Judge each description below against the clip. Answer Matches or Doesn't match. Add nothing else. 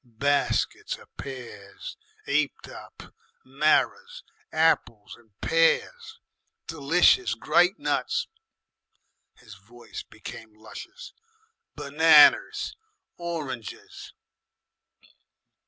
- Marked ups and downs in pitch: Matches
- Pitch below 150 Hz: Matches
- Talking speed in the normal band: Doesn't match